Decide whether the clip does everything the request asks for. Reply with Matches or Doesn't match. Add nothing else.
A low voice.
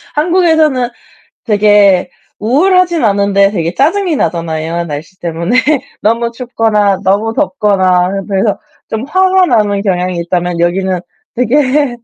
Doesn't match